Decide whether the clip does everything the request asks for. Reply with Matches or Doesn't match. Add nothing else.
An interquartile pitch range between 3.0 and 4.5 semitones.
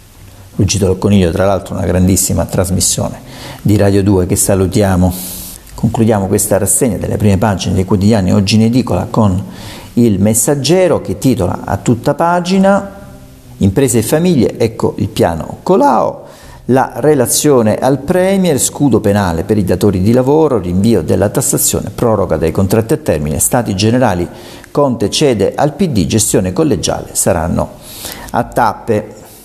Doesn't match